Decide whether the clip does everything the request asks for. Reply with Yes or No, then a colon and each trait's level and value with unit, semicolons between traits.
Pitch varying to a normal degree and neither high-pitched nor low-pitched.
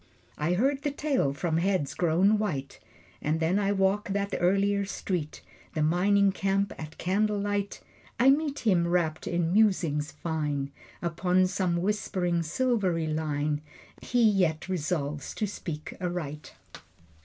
Yes: average, 4.2 semitones; medium, 180 Hz